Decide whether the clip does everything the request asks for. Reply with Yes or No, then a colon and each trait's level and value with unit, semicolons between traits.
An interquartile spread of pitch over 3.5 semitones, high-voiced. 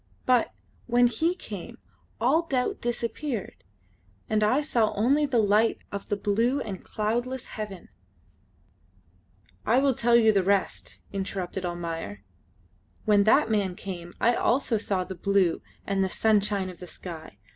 Yes: average, 4.0 semitones; high, 210 Hz